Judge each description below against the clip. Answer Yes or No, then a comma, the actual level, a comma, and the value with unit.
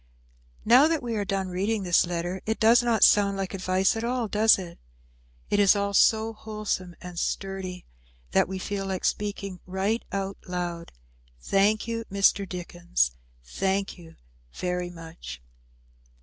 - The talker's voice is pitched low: No, high, 195 Hz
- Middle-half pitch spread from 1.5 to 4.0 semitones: Yes, average, 2.9 semitones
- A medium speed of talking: Yes, average, 150 wpm